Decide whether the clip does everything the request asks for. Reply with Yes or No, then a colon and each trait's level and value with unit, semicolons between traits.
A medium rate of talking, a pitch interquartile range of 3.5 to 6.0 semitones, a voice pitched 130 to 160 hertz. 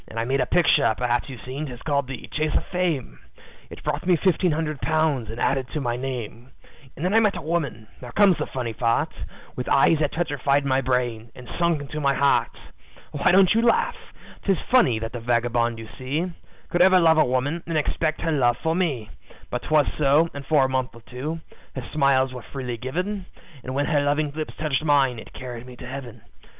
No: fast, 210 wpm; average, 4.2 semitones; medium, 140 Hz